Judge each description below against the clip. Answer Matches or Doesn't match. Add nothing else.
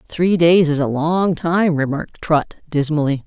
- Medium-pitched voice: Matches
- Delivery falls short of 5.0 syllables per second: Matches